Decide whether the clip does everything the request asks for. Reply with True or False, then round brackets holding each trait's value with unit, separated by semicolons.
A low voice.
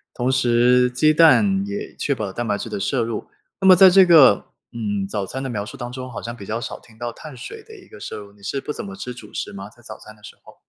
True (120 Hz)